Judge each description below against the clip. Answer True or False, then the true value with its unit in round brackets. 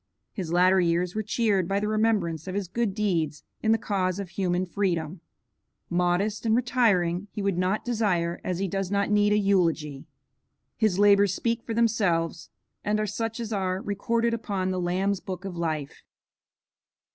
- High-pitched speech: True (195 Hz)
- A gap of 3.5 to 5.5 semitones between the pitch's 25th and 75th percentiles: False (3.1 semitones)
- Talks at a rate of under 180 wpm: True (170 wpm)